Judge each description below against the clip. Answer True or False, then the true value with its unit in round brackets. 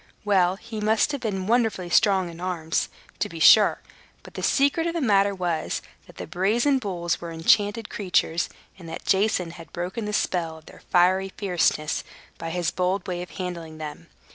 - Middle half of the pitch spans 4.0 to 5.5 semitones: False (3.5 semitones)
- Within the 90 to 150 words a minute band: False (190 wpm)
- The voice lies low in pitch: False (185 Hz)